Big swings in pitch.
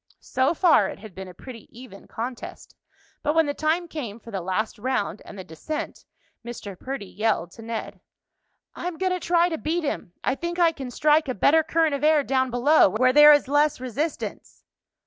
Yes: wide, 5.7 semitones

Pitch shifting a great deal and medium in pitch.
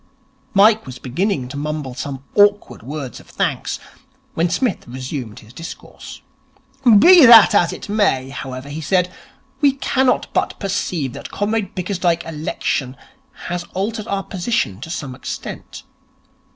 Yes: wide, 7.4 semitones; medium, 170 Hz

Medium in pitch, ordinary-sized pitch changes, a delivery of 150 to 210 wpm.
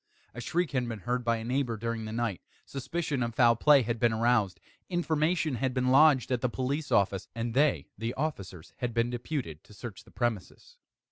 No: low, 120 Hz; average, 3.4 semitones; average, 200 wpm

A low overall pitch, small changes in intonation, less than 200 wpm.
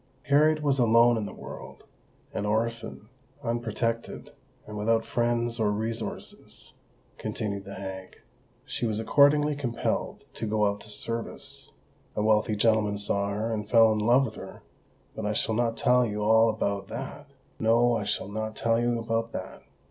Yes: low, 115 Hz; narrow, 2.0 semitones; average, 150 wpm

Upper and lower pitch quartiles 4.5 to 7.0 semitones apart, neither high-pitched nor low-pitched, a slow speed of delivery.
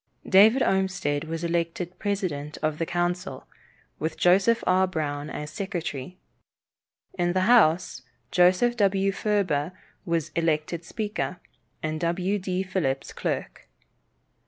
No: average, 3.4 semitones; medium, 180 Hz; slow, 115 wpm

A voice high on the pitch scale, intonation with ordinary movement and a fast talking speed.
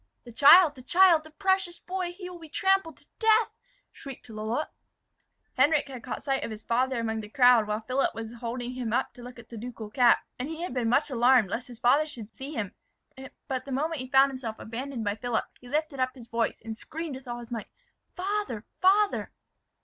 Yes: very high, 255 Hz; average, 5.0 semitones; fast, 215 wpm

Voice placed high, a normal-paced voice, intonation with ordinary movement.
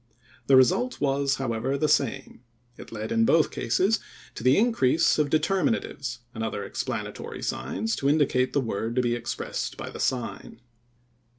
No: low, 135 Hz; average, 160 wpm; average, 4.2 semitones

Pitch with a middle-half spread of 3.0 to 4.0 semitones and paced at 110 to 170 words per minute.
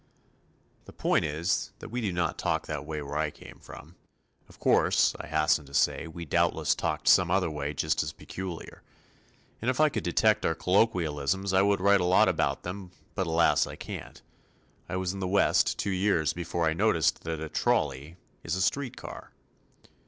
No: average, 3.7 semitones; average, 190 wpm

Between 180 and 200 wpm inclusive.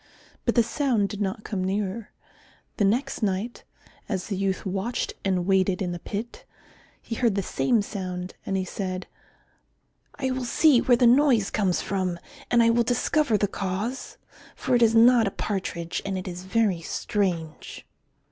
No: average, 170 wpm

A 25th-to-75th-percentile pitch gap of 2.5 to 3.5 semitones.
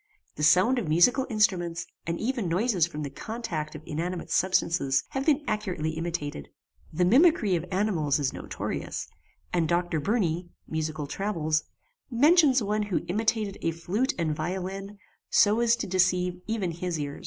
No: average, 5.1 semitones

